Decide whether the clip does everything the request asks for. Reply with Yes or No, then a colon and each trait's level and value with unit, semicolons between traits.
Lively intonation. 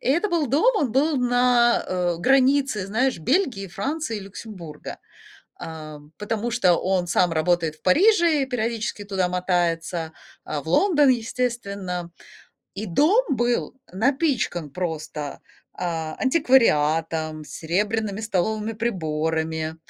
Yes: wide, 7.2 semitones